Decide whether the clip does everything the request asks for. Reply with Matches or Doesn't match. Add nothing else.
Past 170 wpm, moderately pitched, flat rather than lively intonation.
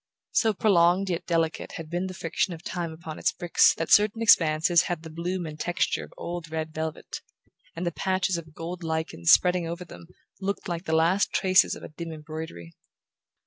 Matches